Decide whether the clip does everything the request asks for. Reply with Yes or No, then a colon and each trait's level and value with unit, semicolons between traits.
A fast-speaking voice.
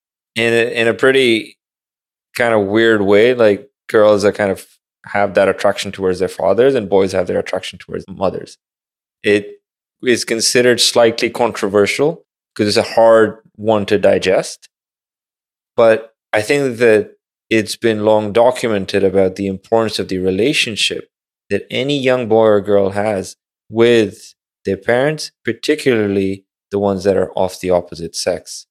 No: average, 150 wpm